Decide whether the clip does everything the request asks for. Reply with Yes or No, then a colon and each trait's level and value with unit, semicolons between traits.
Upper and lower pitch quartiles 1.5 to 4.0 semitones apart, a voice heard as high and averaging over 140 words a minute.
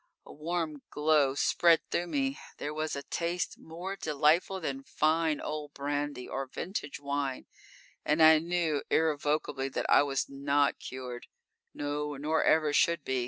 No: narrow, 2.4 semitones; medium, 150 Hz; average, 150 wpm